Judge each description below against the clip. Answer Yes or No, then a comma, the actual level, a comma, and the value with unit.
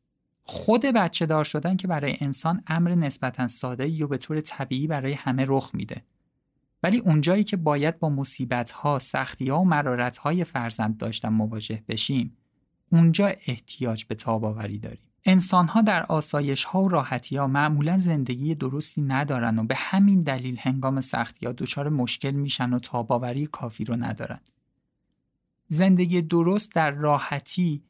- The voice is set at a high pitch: No, medium, 140 Hz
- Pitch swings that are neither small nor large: Yes, average, 5.0 semitones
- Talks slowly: No, fast, 155 wpm